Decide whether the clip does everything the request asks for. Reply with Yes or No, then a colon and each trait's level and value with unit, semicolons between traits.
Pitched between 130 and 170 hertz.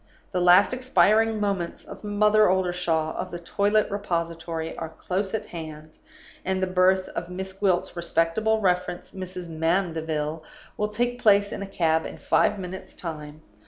No: medium, 185 Hz